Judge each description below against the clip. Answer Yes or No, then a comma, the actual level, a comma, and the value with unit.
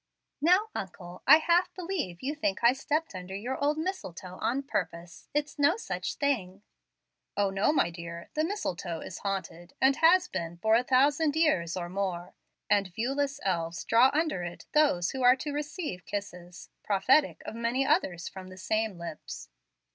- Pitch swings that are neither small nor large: No, wide, 8.5 semitones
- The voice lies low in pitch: No, high, 225 Hz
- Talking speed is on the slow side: No, average, 170 wpm